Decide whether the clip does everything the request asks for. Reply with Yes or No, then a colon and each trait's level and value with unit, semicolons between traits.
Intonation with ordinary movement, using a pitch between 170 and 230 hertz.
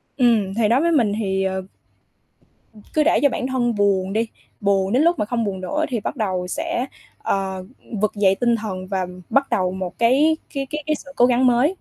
No: wide, 6.0 semitones; high, 225 Hz